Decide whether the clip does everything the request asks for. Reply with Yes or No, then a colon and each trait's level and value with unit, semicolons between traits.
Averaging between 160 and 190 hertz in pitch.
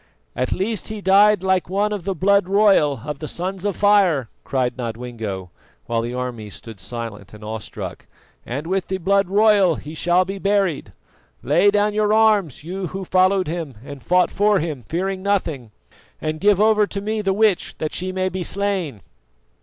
Yes: medium, 185 Hz